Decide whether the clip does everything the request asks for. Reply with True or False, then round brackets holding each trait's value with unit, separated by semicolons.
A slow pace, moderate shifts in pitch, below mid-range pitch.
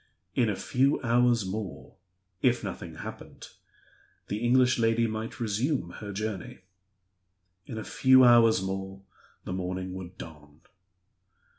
True (125 wpm; 4.1 semitones; 110 Hz)